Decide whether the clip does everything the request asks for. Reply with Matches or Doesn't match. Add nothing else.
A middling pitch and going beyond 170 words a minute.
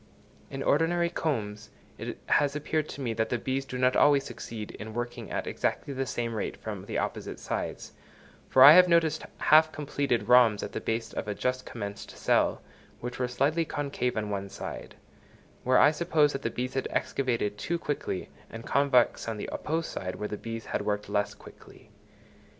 Doesn't match